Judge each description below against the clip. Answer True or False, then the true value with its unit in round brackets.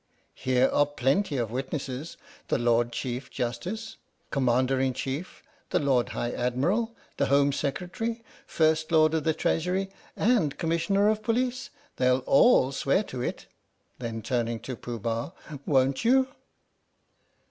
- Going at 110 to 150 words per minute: True (135 wpm)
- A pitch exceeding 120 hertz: True (140 Hz)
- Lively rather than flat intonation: True (6.5 semitones)